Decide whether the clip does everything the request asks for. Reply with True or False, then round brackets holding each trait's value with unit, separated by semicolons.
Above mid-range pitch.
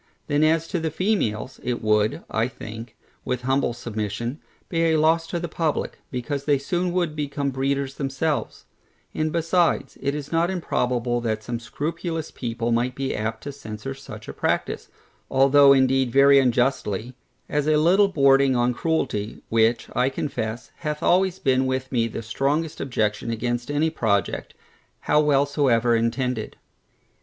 False (135 Hz)